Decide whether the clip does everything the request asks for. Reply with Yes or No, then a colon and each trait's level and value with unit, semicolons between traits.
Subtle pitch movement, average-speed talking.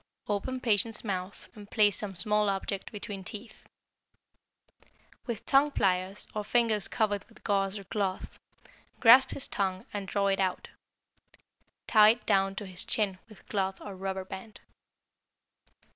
Yes: narrow, 2.0 semitones; average, 145 wpm